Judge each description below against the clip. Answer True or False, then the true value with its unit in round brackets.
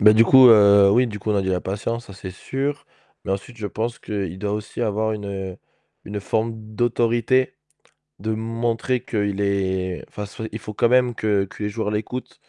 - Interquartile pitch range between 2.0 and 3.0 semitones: True (2.5 semitones)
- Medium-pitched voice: False (105 Hz)